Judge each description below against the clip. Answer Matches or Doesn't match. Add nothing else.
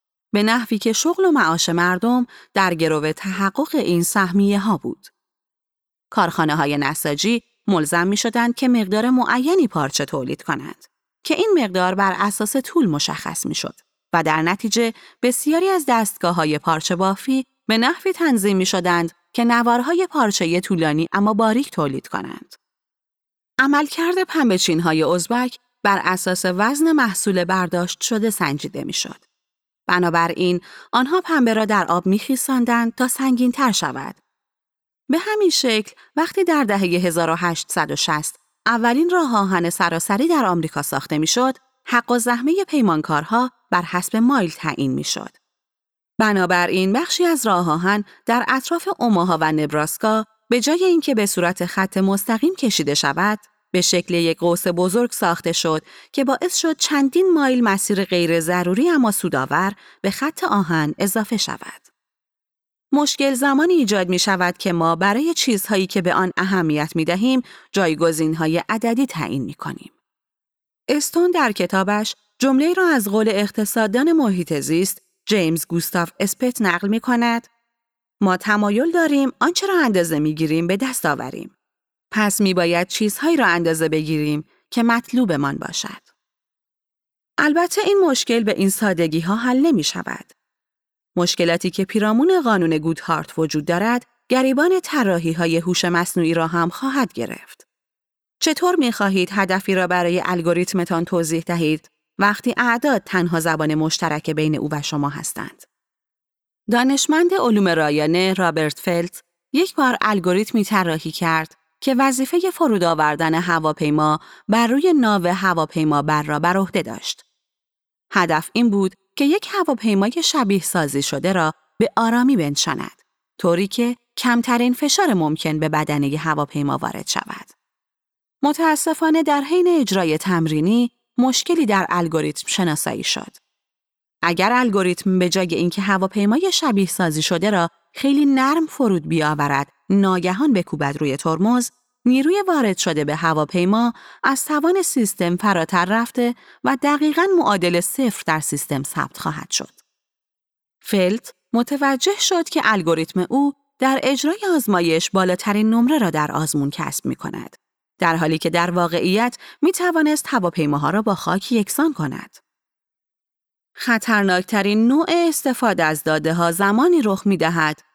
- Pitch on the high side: Matches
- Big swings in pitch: Matches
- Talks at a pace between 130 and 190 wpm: Matches